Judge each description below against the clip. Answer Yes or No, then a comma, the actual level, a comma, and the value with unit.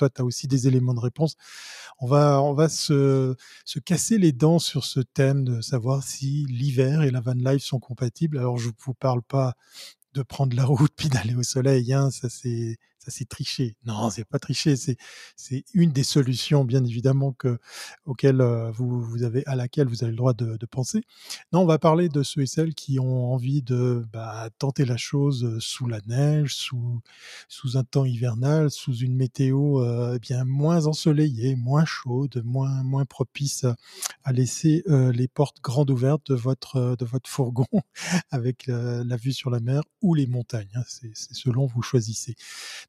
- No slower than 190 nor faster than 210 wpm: Yes, average, 195 wpm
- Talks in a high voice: No, low, 130 Hz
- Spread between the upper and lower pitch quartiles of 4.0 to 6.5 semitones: No, narrow, 2.4 semitones